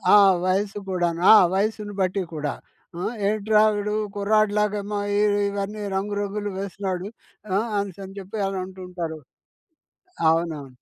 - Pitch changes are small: Yes, narrow, 2.1 semitones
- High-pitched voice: Yes, high, 195 Hz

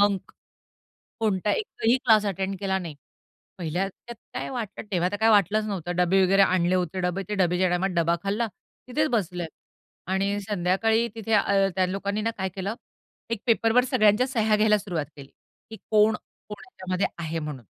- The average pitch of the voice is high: Yes, high, 195 Hz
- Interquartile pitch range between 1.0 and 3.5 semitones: Yes, average, 3.1 semitones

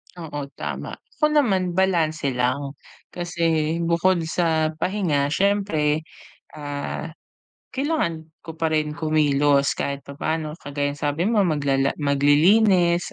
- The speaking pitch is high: No, medium, 160 Hz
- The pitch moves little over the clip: No, average, 3.4 semitones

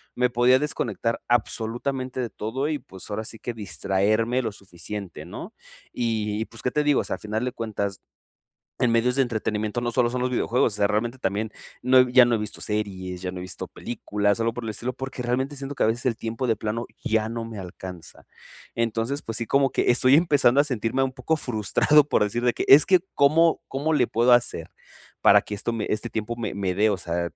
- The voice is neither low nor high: No, low, 115 Hz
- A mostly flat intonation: No, average, 3.1 semitones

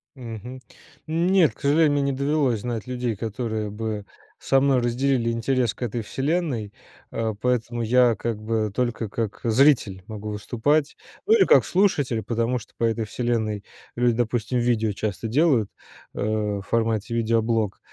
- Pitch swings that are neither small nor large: Yes, average, 3.1 semitones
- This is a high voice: No, low, 115 Hz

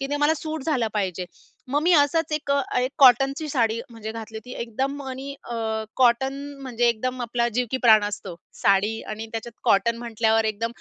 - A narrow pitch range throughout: No, average, 3.7 semitones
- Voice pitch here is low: No, high, 240 Hz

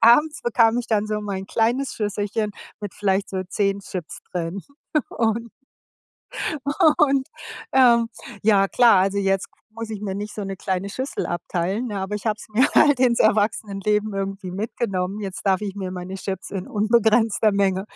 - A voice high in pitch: Yes, high, 205 Hz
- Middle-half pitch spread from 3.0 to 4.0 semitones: No, narrow, 2.6 semitones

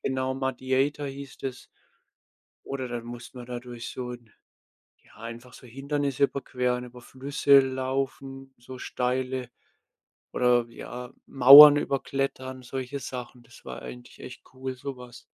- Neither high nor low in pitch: No, low, 130 Hz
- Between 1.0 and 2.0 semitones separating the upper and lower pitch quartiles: Yes, narrow, 1.6 semitones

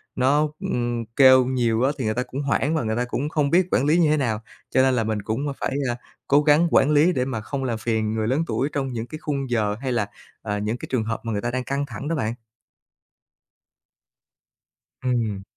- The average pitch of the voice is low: Yes, low, 125 Hz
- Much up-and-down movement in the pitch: No, average, 3.9 semitones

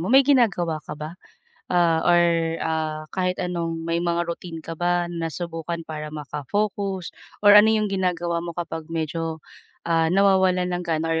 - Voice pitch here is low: No, medium, 170 Hz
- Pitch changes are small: Yes, narrow, 1.9 semitones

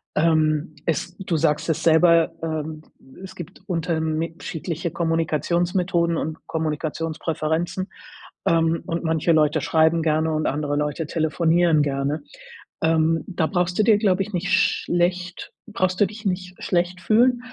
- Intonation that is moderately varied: No, narrow, 2.2 semitones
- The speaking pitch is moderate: Yes, medium, 165 Hz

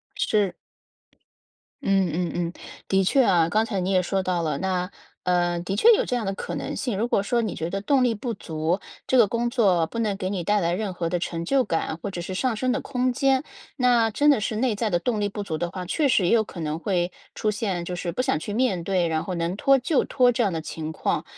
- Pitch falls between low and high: No, high, 195 Hz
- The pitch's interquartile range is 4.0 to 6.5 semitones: Yes, average, 5.1 semitones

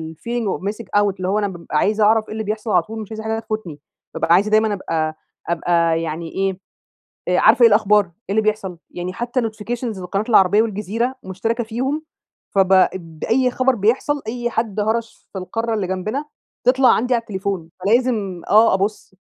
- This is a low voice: No, high, 210 Hz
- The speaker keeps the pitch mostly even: No, average, 3.4 semitones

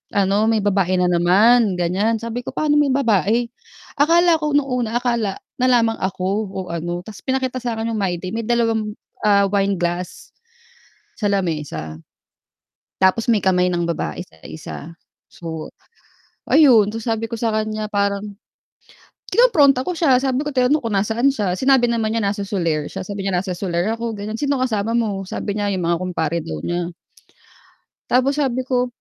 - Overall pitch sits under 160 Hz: No, high, 215 Hz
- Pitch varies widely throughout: No, average, 4.7 semitones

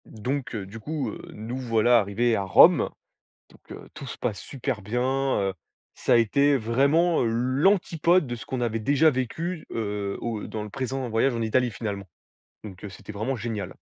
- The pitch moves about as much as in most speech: Yes, average, 4.0 semitones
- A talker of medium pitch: No, low, 120 Hz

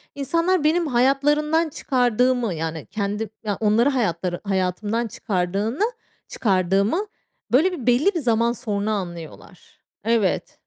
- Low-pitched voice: No, high, 230 Hz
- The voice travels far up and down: Yes, wide, 5.8 semitones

